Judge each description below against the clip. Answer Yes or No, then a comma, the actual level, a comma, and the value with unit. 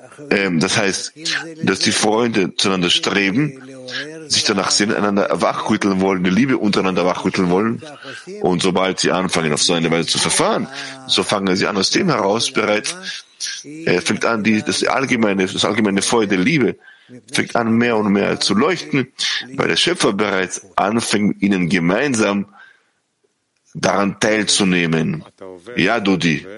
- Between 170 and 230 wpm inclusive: No, average, 150 wpm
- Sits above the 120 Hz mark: No, low, 100 Hz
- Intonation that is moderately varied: Yes, average, 3.1 semitones